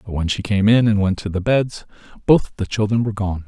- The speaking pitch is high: No, low, 105 Hz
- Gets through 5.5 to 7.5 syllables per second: Yes, 5.9 syllables/s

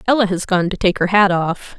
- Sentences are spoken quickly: Yes, fast, 270 wpm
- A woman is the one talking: Yes, female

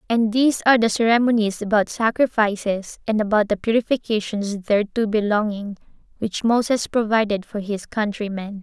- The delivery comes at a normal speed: No, slow, 130 wpm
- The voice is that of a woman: Yes, female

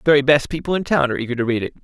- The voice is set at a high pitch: No, medium, 140 Hz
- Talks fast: Yes, fast, 360 wpm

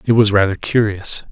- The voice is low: Yes, low, 105 Hz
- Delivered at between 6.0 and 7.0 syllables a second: No, 5.1 syllables/s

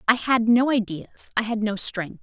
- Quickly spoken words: Yes, fast, 215 wpm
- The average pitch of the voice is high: Yes, high, 225 Hz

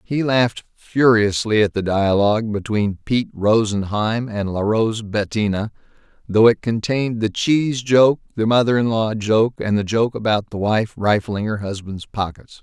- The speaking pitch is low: Yes, low, 110 Hz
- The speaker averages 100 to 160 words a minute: Yes, average, 155 wpm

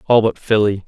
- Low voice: Yes, low, 105 Hz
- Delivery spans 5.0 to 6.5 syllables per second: Yes, 5.3 syllables/s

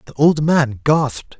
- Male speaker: Yes, male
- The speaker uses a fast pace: No, average, 170 wpm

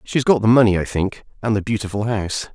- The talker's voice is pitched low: Yes, low, 110 Hz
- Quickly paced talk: Yes, fast, 235 wpm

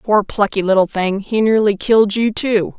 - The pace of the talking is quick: No, average, 195 wpm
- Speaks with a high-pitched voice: Yes, high, 205 Hz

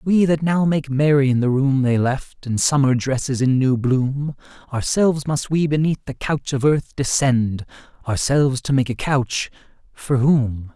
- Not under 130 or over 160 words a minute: No, average, 180 wpm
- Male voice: Yes, male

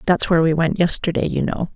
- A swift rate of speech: Yes, fast, 240 wpm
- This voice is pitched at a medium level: Yes, medium, 165 Hz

